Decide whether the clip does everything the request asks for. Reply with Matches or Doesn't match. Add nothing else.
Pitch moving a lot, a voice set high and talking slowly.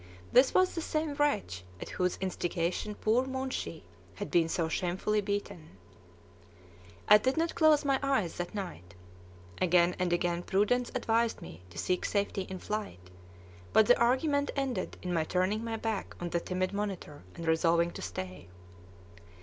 Doesn't match